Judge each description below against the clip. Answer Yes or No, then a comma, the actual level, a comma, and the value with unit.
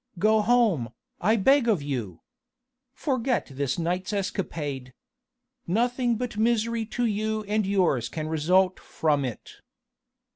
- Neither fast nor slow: No, slow, 120 wpm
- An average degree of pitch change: No, wide, 6.8 semitones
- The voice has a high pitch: Yes, high, 200 Hz